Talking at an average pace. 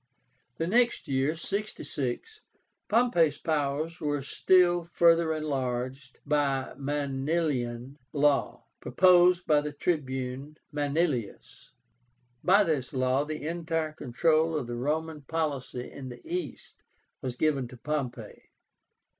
No: slow, 115 wpm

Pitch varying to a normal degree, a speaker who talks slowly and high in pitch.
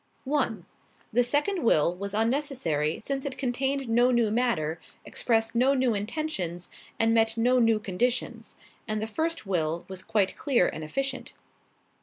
No: average, 5.0 semitones; average, 150 wpm; high, 230 Hz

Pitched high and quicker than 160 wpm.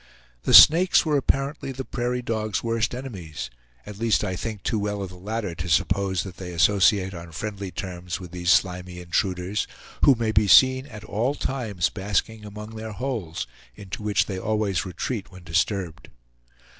No: low, 100 Hz; average, 170 wpm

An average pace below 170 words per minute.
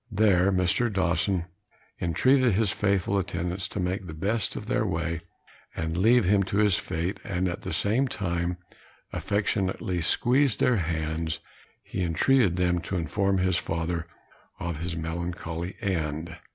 Yes: average, 145 wpm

